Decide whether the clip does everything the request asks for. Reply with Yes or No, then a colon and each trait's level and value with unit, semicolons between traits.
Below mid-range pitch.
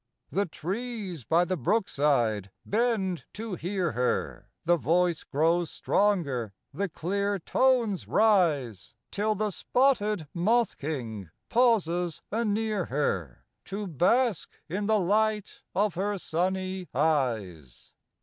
No: medium, 185 Hz